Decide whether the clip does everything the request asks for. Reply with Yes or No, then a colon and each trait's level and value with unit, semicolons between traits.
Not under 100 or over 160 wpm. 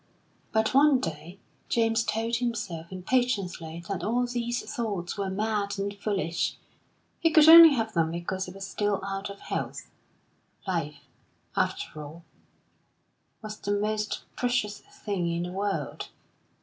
Yes: slow, 135 wpm